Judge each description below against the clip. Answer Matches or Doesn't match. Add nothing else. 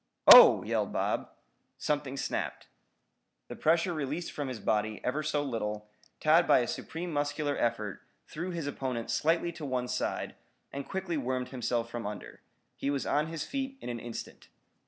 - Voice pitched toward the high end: Doesn't match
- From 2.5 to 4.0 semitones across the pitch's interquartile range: Doesn't match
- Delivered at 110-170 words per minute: Matches